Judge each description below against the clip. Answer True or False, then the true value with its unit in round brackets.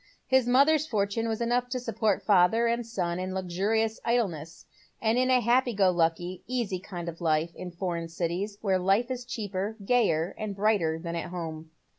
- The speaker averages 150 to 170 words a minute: False (185 wpm)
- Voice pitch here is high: True (200 Hz)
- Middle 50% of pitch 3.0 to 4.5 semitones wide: False (5.2 semitones)